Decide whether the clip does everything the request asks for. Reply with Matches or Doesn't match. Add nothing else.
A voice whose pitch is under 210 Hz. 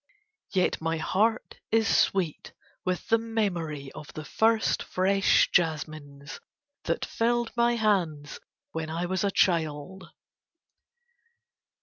Matches